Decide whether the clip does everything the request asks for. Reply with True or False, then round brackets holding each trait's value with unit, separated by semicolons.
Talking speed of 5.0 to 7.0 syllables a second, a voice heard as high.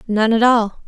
False (4.5 syllables/s; 225 Hz)